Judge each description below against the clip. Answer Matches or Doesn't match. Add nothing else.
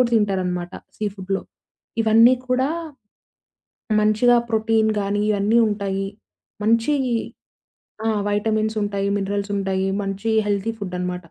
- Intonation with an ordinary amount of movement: Doesn't match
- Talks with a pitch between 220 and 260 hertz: Doesn't match